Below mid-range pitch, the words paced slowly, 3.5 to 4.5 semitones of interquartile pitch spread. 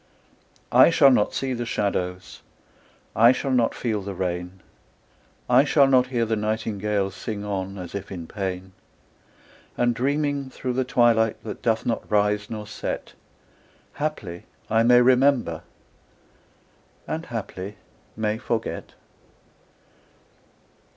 Yes: low, 110 Hz; slow, 125 wpm; average, 4.0 semitones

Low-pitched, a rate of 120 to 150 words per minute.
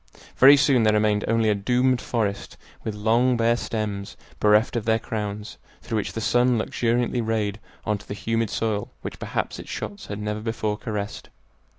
No: low, 110 Hz; average, 180 wpm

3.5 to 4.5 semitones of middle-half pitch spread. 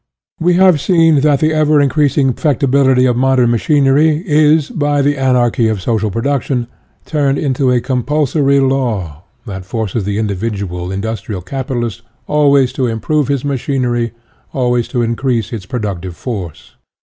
Yes: average, 4.2 semitones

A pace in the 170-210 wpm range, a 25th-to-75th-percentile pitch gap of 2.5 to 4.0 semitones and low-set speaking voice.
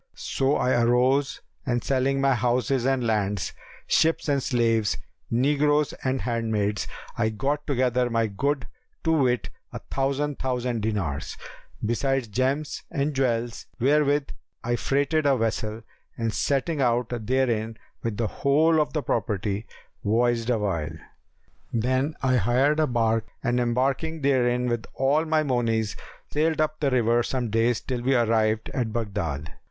No: average, 140 wpm; average, 3.3 semitones; low, 125 Hz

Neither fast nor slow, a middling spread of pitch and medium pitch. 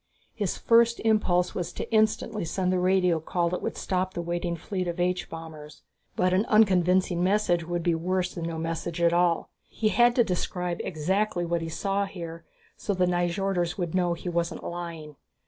No: average, 185 wpm; narrow, 1.9 semitones; medium, 180 Hz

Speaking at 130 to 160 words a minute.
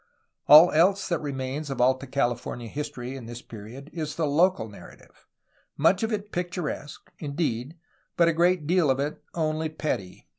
No: average, 170 wpm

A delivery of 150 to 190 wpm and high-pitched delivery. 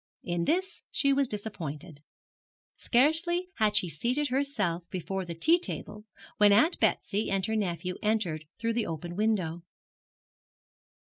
No: slow, 135 wpm; high, 210 Hz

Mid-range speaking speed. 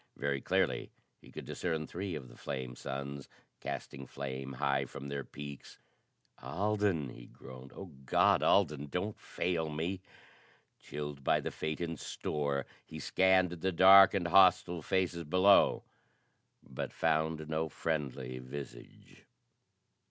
No: slow, 130 wpm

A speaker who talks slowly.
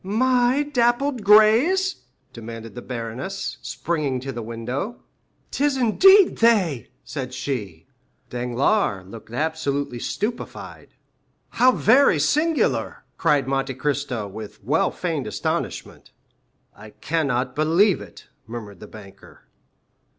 Yes: slow, 105 wpm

